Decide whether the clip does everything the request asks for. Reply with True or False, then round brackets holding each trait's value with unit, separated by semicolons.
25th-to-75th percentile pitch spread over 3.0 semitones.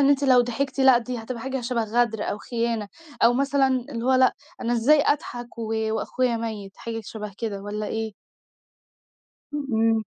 False (2.7 semitones)